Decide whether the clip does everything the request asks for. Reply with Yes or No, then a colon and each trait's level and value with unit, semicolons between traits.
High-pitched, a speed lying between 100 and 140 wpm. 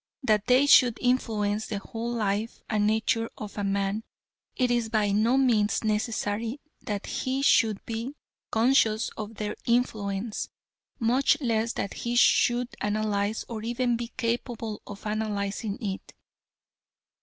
Yes: high, 220 Hz; slow, 135 wpm